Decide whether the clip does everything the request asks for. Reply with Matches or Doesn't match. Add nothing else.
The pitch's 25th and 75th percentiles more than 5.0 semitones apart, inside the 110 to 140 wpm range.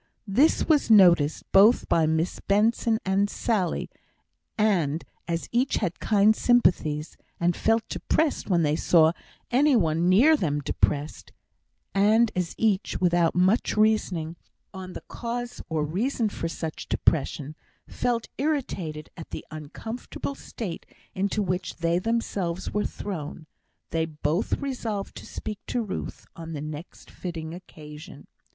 Matches